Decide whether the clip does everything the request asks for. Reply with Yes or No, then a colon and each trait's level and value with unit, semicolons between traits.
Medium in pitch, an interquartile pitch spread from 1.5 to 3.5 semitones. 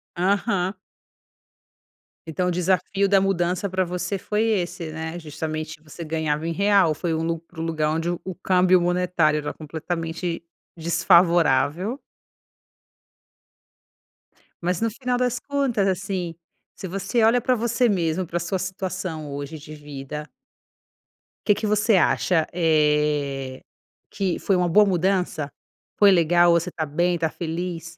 Yes: medium, 175 Hz; average, 3.2 semitones